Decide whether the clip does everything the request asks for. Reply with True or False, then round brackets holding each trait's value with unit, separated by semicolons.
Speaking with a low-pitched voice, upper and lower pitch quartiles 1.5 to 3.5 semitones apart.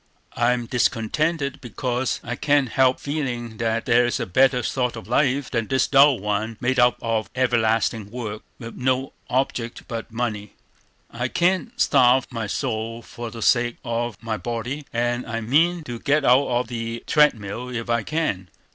True (120 Hz; 2.4 semitones)